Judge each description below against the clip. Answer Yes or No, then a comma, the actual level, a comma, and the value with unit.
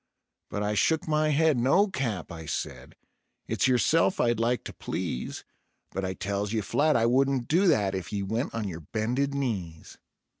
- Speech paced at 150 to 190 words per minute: Yes, average, 180 wpm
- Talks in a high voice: No, low, 115 Hz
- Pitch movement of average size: No, wide, 5.8 semitones